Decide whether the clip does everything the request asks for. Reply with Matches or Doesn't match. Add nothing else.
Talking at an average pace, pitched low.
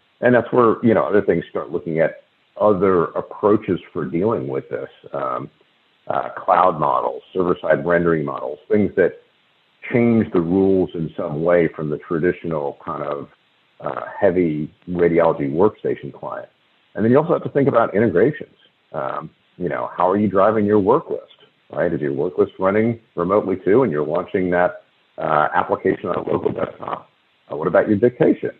Matches